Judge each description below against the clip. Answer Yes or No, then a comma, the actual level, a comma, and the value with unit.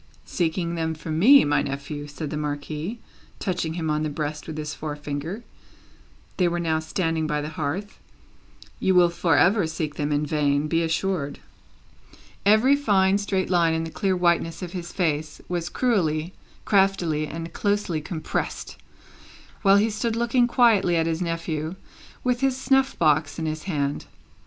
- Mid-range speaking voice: Yes, medium, 165 Hz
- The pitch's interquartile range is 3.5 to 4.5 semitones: Yes, average, 4.0 semitones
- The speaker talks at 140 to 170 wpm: Yes, average, 160 wpm